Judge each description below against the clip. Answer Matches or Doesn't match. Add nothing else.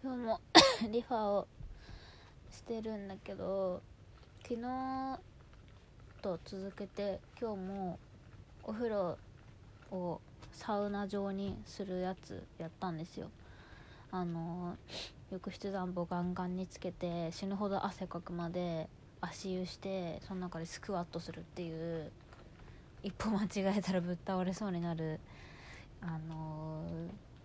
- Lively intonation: Doesn't match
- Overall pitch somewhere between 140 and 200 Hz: Matches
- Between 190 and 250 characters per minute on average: Matches